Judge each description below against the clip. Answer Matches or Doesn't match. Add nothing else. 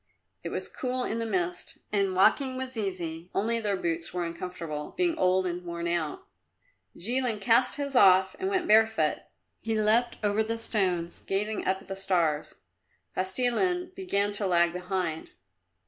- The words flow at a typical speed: Matches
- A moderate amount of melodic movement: Matches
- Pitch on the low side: Doesn't match